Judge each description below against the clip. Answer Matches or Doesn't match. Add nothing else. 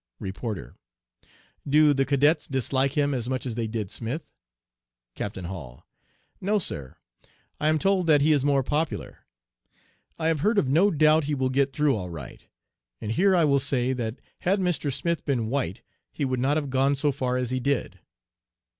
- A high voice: Doesn't match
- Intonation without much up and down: Doesn't match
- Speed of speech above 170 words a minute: Matches